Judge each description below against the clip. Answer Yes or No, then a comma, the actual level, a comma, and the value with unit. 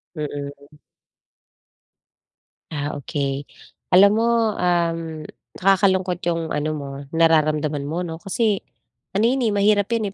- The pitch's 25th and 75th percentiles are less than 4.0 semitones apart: No, average, 4.5 semitones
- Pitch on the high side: No, medium, 165 Hz